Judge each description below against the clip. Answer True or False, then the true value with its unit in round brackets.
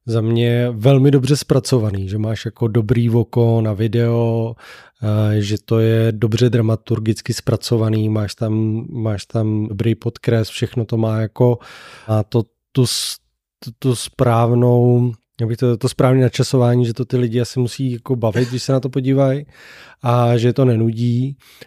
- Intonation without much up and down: True (1.8 semitones)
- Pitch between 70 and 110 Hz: False (120 Hz)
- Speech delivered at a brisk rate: False (155 wpm)